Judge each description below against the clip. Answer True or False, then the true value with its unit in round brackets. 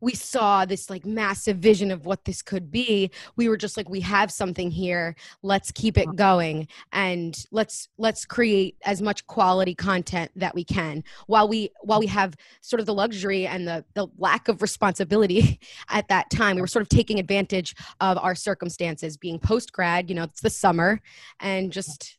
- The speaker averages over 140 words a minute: True (190 wpm)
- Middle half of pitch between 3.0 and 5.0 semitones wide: False (2.5 semitones)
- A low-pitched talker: False (195 Hz)